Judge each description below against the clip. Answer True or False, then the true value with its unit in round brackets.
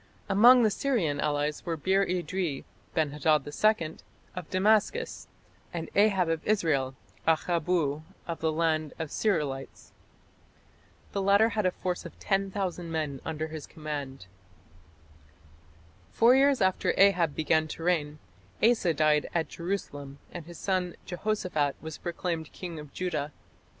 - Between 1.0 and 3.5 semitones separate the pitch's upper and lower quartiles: False (4.2 semitones)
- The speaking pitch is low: False (170 Hz)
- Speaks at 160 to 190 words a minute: False (135 wpm)